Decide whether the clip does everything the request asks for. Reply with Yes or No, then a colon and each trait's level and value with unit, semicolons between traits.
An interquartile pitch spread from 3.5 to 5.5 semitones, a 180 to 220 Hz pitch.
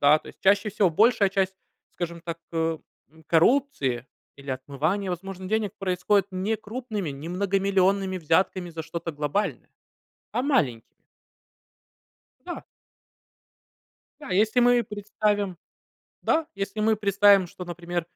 Yes: average, 3.8 semitones; high, 190 Hz